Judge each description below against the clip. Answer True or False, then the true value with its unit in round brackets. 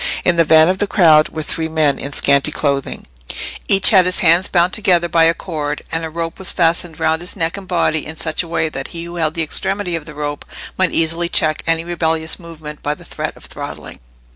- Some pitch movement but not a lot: False (1.9 semitones)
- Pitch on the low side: False (165 Hz)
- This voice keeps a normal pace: False (230 wpm)